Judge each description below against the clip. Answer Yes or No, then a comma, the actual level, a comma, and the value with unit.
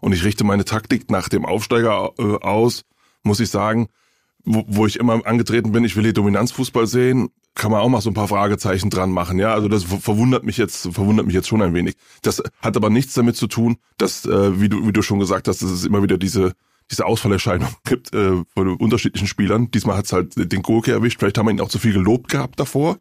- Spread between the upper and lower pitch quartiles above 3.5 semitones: No, narrow, 2.6 semitones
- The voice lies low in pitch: Yes, low, 105 Hz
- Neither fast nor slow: No, fast, 230 wpm